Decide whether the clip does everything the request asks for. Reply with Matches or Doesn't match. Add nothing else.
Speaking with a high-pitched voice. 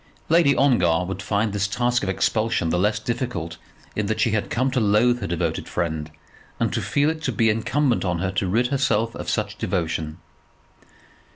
Doesn't match